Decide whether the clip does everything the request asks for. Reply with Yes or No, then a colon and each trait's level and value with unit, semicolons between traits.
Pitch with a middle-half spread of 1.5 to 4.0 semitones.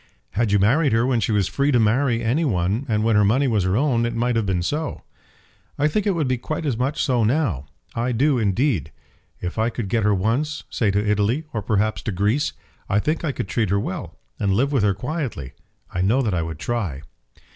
No: average, 4.9 semitones